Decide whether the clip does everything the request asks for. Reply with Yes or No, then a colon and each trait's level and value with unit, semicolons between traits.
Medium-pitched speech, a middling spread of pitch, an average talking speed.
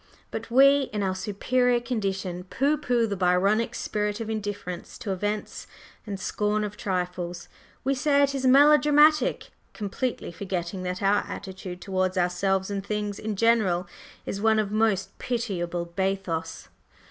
No: high, 205 Hz; average, 3.9 semitones; average, 145 wpm